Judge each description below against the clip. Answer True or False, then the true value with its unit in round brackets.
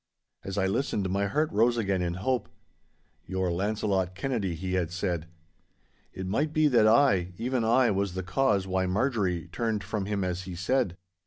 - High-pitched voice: False (100 Hz)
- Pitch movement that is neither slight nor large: True (3.9 semitones)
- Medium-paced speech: True (175 wpm)